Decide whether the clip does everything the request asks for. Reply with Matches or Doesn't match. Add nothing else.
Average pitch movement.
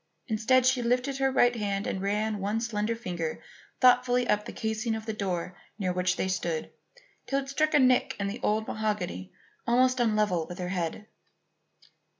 Matches